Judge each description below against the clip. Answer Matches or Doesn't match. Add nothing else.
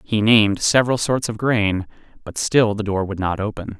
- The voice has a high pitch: Doesn't match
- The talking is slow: Doesn't match